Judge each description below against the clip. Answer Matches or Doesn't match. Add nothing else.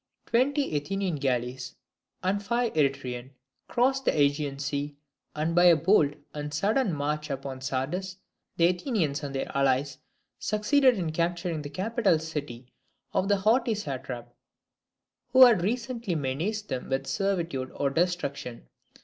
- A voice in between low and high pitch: Matches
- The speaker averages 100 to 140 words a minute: Matches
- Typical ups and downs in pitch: Doesn't match